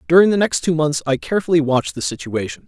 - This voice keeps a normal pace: No, fast, 225 wpm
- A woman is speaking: No, male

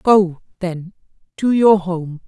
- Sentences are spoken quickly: No, slow, 130 wpm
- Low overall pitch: No, medium, 185 Hz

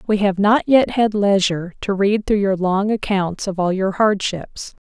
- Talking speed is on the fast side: No, average, 195 wpm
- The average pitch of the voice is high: Yes, high, 200 Hz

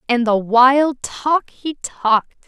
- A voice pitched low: No, very high, 255 Hz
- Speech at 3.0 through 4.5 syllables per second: Yes, 3.4 syllables/s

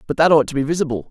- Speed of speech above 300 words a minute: Yes, fast, 325 wpm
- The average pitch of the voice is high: No, medium, 145 Hz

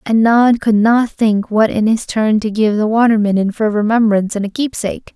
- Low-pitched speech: No, high, 220 Hz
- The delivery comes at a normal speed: No, fast, 235 wpm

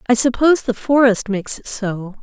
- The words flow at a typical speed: Yes, average, 190 wpm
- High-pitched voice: Yes, high, 230 Hz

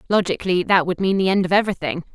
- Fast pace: Yes, fast, 225 wpm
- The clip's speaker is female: Yes, female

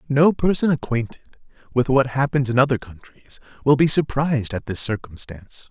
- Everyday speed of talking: Yes, average, 160 wpm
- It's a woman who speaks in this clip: No, male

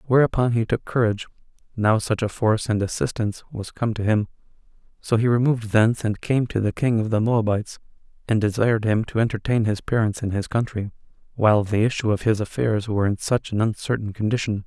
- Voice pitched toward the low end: Yes, low, 110 Hz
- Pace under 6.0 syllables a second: No, 6.1 syllables/s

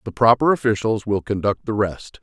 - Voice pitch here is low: Yes, low, 110 Hz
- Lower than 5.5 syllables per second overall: Yes, 5.2 syllables/s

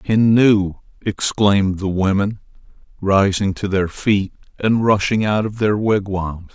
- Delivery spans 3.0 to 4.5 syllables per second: Yes, 4.0 syllables/s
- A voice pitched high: No, low, 100 Hz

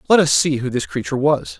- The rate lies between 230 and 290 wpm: Yes, fast, 265 wpm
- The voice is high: No, medium, 145 Hz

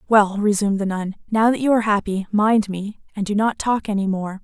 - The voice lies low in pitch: No, high, 205 Hz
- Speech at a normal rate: No, fast, 230 wpm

